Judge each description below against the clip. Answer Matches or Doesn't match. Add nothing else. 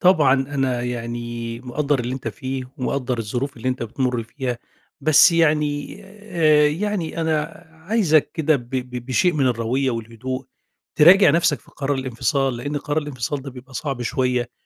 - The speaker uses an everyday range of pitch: Matches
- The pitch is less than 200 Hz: Matches